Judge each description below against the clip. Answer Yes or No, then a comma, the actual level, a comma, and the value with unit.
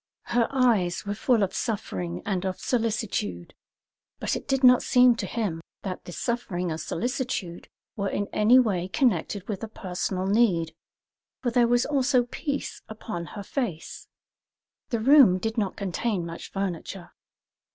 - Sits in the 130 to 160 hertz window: No, high, 210 Hz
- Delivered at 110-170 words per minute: Yes, average, 150 wpm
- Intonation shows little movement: No, average, 5.1 semitones